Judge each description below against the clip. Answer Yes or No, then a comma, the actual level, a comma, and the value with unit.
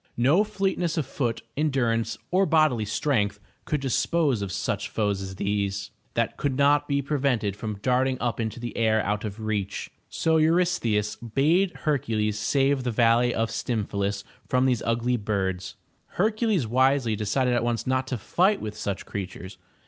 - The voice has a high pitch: No, low, 120 Hz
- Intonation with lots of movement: No, average, 5.0 semitones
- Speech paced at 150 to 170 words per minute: Yes, average, 165 wpm